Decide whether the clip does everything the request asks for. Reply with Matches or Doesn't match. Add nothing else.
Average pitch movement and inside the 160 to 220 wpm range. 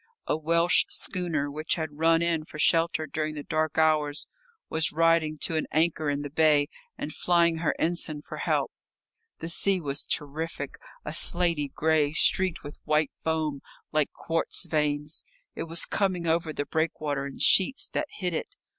Doesn't match